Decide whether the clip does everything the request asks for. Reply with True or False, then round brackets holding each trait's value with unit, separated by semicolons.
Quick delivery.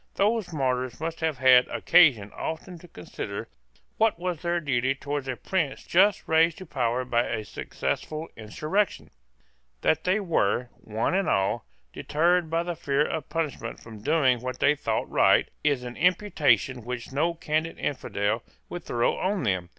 False (160 wpm)